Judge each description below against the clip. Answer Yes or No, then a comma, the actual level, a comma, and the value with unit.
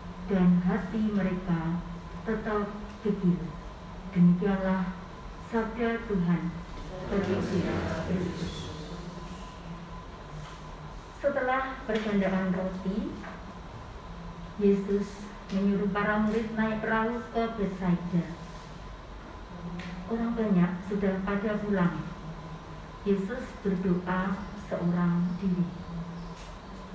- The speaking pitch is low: No, high, 195 Hz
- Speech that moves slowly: Yes, slow, 65 wpm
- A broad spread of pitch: No, average, 3.0 semitones